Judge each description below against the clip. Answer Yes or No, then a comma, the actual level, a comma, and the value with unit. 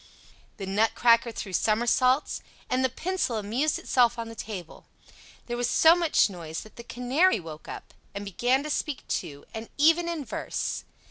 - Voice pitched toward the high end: Yes, high, 240 Hz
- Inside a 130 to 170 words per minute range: Yes, average, 165 wpm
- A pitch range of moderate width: Yes, average, 4.9 semitones